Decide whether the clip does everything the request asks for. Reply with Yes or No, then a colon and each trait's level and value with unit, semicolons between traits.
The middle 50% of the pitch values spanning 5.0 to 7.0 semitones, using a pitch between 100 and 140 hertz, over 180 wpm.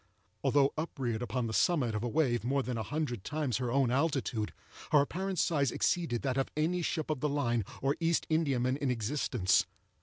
No: average, 4.2 semitones; low, 135 Hz; average, 190 wpm